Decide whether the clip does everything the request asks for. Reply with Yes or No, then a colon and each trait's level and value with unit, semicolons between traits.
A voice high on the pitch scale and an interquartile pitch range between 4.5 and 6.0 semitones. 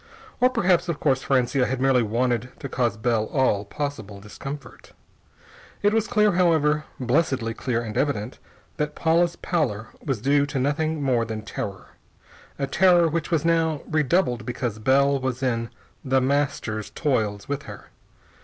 No: low, 135 Hz; average, 4.9 semitones